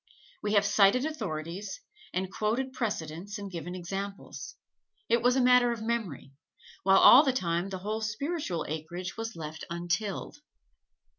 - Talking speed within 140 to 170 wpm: Yes, average, 145 wpm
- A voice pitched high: Yes, high, 200 Hz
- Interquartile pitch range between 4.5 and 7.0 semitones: Yes, average, 5.1 semitones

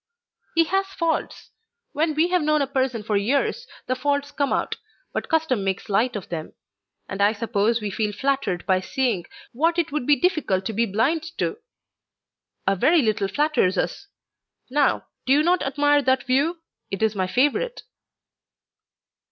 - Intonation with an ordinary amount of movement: No, wide, 6.7 semitones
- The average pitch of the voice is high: Yes, very high, 265 Hz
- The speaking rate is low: No, average, 170 wpm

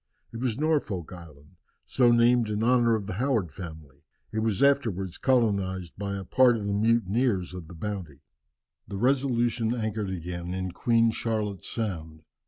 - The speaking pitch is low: Yes, low, 105 Hz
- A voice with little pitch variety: No, average, 4.4 semitones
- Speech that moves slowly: No, average, 160 wpm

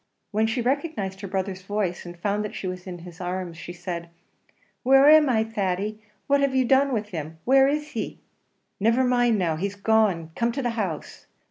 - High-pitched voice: Yes, high, 210 Hz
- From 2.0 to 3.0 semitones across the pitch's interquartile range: No, wide, 5.4 semitones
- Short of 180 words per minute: No, average, 200 wpm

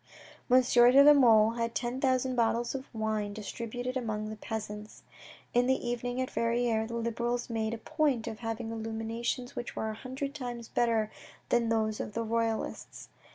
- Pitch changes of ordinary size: No, narrow, 1.8 semitones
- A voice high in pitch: Yes, high, 235 Hz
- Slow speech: No, average, 170 wpm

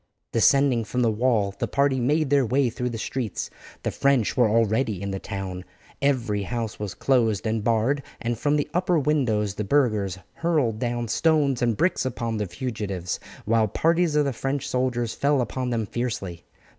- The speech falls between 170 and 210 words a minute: Yes, average, 180 wpm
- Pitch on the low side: Yes, low, 120 Hz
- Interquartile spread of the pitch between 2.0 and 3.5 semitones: No, average, 4.2 semitones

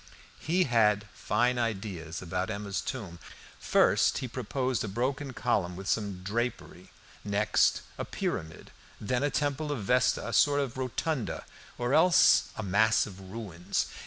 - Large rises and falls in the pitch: No, average, 4.7 semitones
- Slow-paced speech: No, average, 145 wpm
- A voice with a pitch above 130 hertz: No, low, 110 Hz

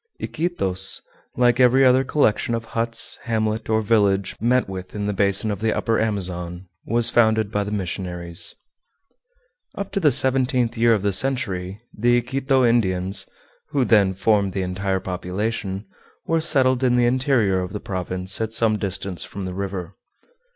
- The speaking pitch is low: Yes, low, 110 Hz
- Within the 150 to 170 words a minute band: Yes, average, 160 wpm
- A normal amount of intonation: Yes, average, 4.2 semitones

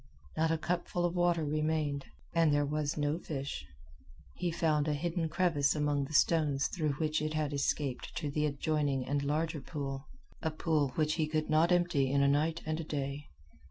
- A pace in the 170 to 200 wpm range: Yes, average, 190 wpm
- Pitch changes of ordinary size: No, narrow, 2.1 semitones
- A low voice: No, medium, 155 Hz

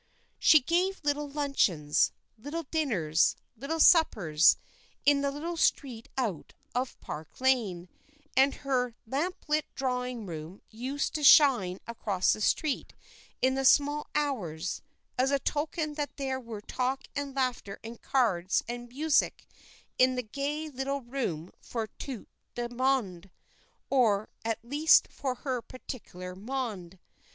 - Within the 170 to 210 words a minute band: No, slow, 135 wpm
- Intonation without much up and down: No, average, 4.8 semitones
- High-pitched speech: Yes, very high, 255 Hz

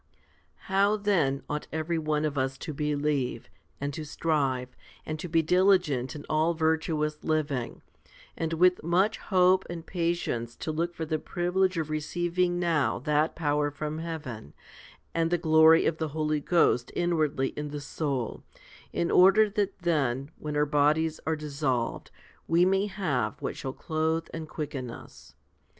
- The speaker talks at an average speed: Yes, average, 160 wpm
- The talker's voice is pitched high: No, medium, 155 Hz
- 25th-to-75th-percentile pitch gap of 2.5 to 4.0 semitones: Yes, average, 2.8 semitones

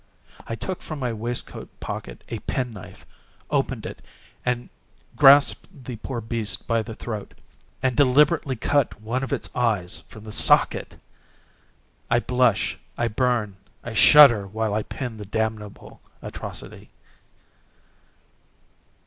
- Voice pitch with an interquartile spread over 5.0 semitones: No, average, 3.2 semitones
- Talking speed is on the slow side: Yes, slow, 125 wpm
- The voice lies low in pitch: Yes, low, 115 Hz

